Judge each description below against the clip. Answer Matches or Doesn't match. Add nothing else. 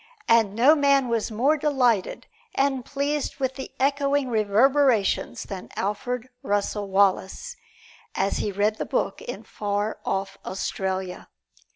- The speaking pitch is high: Matches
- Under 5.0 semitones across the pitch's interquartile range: Doesn't match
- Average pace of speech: Doesn't match